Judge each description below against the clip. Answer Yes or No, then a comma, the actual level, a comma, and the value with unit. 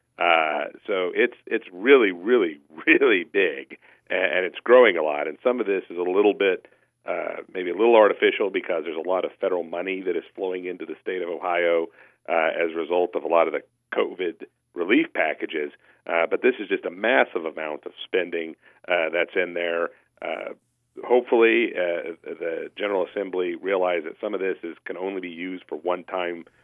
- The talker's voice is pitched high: Yes, very high, 390 Hz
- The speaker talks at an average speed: Yes, average, 195 wpm